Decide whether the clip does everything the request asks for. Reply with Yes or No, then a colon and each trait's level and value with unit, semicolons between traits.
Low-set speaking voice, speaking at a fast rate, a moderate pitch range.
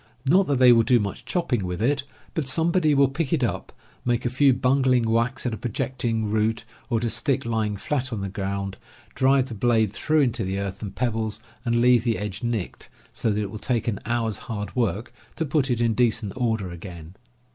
Yes: low, 120 Hz; fast, 215 wpm; average, 3.5 semitones